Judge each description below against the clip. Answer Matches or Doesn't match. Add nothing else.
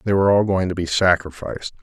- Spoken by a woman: Doesn't match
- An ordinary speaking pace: Doesn't match